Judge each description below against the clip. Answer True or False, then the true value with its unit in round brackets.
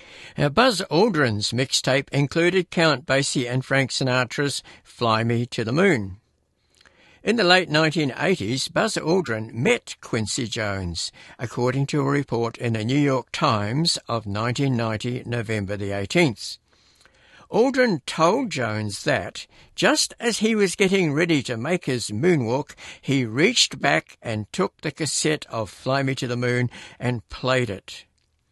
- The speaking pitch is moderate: False (130 Hz)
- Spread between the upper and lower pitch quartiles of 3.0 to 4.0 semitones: False (5.3 semitones)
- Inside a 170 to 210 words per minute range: False (145 wpm)